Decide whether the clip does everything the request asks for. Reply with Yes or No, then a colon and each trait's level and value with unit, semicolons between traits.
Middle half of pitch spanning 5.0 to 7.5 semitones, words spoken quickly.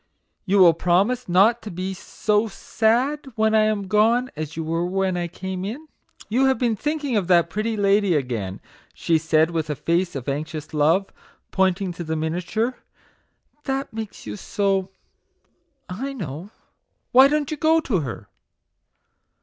No: average, 5.3 semitones; average, 165 wpm